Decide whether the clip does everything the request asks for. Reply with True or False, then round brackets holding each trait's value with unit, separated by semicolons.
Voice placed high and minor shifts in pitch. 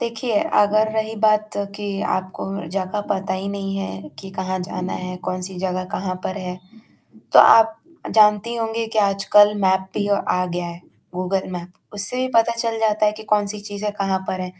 True (200 Hz; 2.3 semitones)